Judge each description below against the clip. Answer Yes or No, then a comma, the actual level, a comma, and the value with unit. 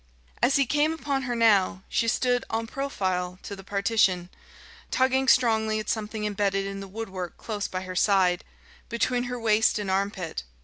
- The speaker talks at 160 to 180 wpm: Yes, average, 170 wpm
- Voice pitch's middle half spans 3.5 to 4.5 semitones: Yes, average, 4.0 semitones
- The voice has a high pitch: Yes, high, 215 Hz